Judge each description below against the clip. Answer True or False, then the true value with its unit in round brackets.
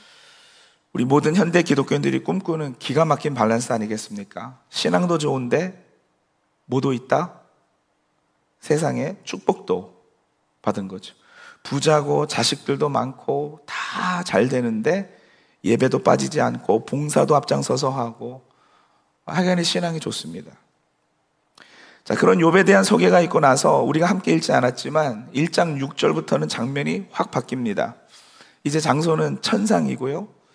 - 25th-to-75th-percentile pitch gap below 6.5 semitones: False (6.9 semitones)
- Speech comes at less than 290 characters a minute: True (270 characters per minute)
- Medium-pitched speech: True (145 Hz)